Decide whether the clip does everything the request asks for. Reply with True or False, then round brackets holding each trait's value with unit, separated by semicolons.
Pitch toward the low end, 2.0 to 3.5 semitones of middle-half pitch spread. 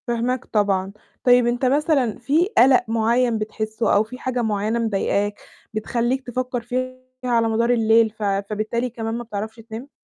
False (230 Hz; 2.4 semitones)